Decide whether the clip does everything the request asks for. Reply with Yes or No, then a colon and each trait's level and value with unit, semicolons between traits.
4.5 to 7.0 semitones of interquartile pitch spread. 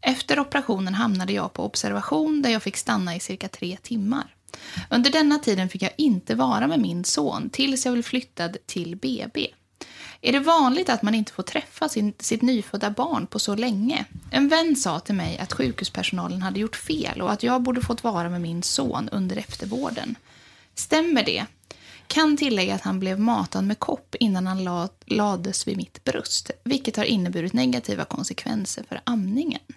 Yes: wide, 5.5 semitones